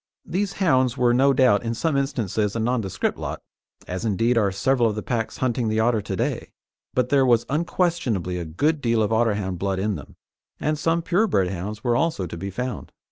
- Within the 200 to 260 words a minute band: Yes, fast, 205 wpm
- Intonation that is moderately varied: Yes, average, 4.8 semitones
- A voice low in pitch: Yes, low, 115 Hz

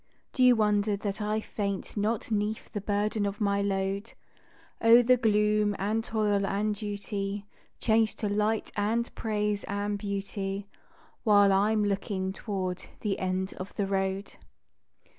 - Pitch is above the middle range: Yes, high, 205 Hz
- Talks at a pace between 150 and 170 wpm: No, average, 140 wpm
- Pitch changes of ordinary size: No, narrow, 1.3 semitones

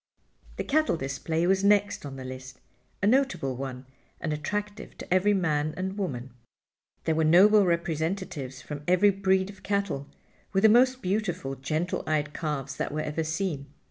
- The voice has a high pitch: No, medium, 170 Hz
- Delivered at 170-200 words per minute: No, average, 160 wpm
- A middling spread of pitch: No, wide, 5.8 semitones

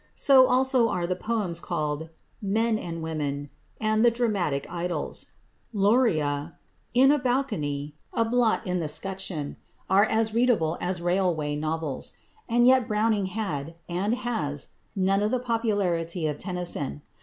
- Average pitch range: No, wide, 6.1 semitones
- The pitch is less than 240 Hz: Yes, high, 190 Hz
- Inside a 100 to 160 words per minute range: Yes, average, 140 wpm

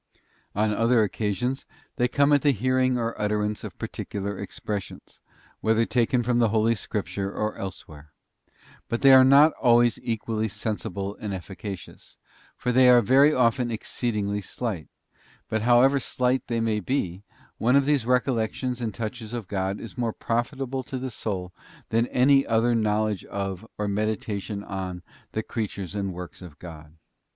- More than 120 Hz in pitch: No, low, 110 Hz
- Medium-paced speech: Yes, average, 160 wpm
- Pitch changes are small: No, average, 3.5 semitones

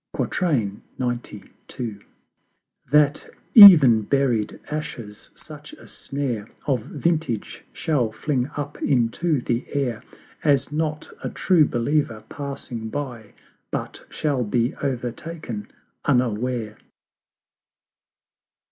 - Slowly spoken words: Yes, slow, 90 wpm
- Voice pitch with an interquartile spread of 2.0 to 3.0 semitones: No, average, 4.4 semitones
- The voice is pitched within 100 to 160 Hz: Yes, low, 135 Hz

